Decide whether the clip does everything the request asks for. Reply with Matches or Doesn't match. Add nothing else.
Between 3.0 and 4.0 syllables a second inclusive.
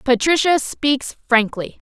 Matches